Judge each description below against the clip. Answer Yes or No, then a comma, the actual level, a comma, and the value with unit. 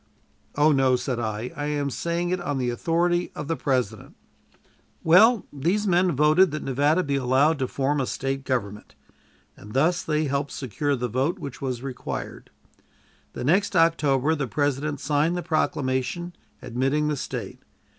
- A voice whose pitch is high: No, medium, 145 Hz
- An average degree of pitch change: Yes, average, 3.9 semitones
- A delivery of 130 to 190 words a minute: Yes, average, 160 wpm